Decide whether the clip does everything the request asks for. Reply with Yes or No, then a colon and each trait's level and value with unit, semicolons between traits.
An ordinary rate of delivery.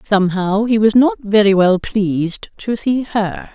Yes: average, 170 wpm